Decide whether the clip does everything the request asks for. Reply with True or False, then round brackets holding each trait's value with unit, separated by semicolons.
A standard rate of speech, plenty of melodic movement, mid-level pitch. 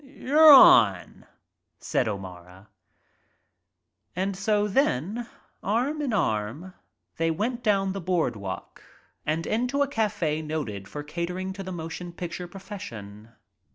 False (120 wpm; 6.8 semitones; 180 Hz)